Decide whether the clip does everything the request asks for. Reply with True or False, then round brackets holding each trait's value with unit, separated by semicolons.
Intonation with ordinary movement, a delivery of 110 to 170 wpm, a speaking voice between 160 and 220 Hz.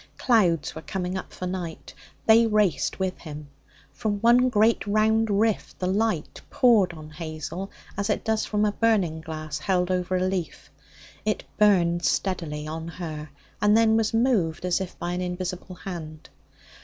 True (4.4 semitones; 165 wpm; 185 Hz)